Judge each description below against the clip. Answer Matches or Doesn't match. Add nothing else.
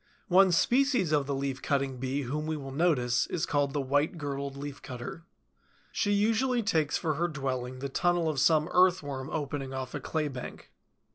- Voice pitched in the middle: Matches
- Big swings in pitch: Doesn't match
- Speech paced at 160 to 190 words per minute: Matches